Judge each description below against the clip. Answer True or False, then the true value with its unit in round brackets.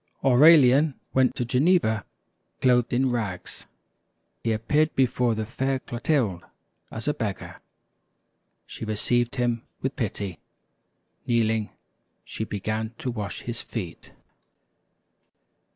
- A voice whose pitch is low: True (120 Hz)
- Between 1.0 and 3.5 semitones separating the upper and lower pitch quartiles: True (3.2 semitones)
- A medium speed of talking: False (105 wpm)